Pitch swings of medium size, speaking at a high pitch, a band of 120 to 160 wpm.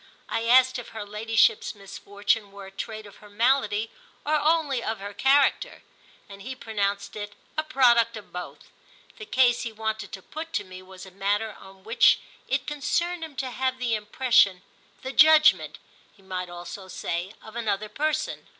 No: average, 4.6 semitones; high, 220 Hz; average, 170 wpm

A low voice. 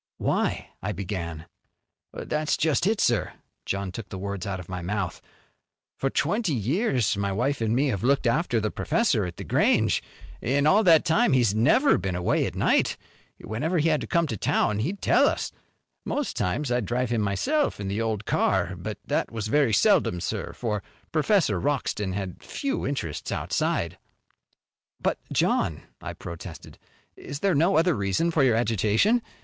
Yes: low, 120 Hz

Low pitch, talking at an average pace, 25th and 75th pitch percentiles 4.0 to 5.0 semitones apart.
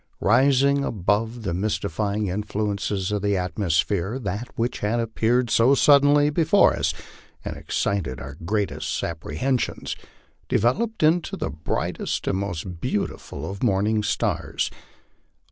No: low, 105 Hz; slow, 125 wpm; average, 4.6 semitones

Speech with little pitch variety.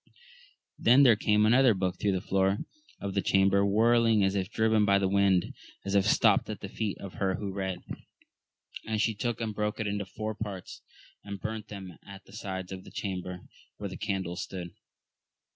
Yes: narrow, 2.1 semitones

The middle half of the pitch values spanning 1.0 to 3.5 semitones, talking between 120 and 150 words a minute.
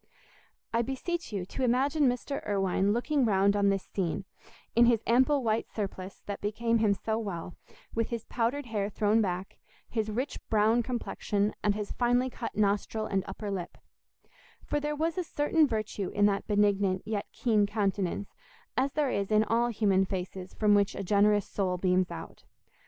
No: average, 3.2 semitones; average, 175 wpm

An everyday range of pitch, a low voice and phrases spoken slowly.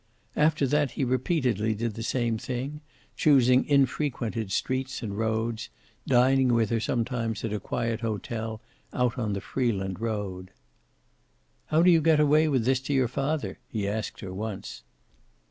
No: average, 3.4 semitones; low, 120 Hz; average, 155 wpm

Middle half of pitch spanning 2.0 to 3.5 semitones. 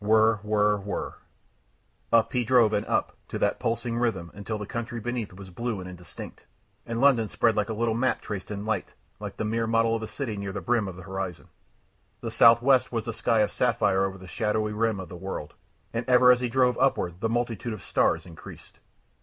Yes: average, 2.8 semitones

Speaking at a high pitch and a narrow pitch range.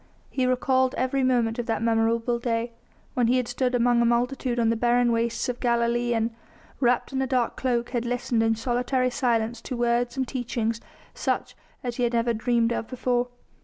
Yes: high, 240 Hz; narrow, 1.2 semitones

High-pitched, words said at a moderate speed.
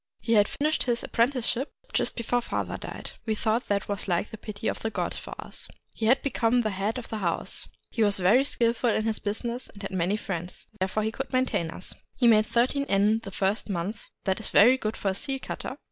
No: high, 220 Hz; fast, 230 wpm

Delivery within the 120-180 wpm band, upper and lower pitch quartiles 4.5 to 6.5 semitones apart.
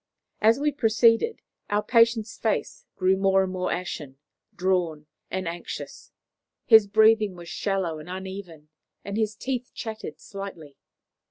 No: slow, 135 wpm; average, 3.7 semitones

